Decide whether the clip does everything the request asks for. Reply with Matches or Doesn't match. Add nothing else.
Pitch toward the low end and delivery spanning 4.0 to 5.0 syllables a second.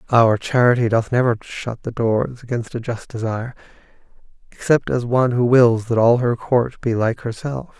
Matches